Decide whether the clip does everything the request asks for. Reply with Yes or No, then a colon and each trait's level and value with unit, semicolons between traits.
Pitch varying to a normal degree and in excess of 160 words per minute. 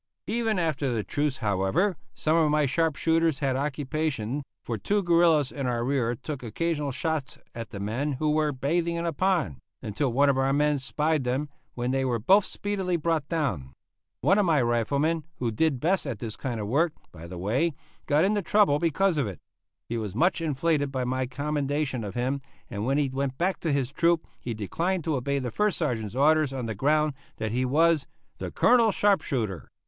Yes: average, 4.8 semitones; average, 200 wpm